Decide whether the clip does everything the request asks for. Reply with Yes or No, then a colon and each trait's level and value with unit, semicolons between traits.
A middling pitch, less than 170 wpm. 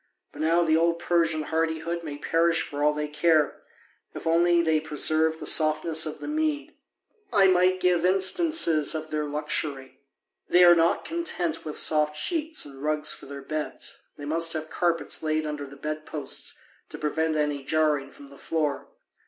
No: medium, 155 Hz; average, 175 wpm